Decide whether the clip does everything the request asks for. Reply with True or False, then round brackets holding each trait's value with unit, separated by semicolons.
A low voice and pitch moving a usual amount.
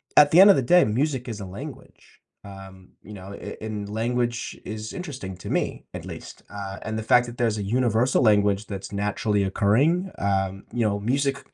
True (110 Hz; 3.8 semitones)